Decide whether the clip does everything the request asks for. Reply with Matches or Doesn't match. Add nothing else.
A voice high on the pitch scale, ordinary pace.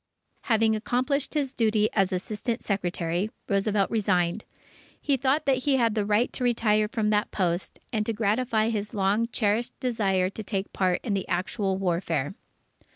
Matches